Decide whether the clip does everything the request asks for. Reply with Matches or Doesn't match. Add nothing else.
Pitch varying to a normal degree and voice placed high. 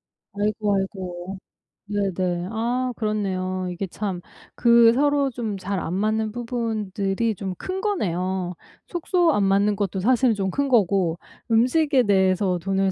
Matches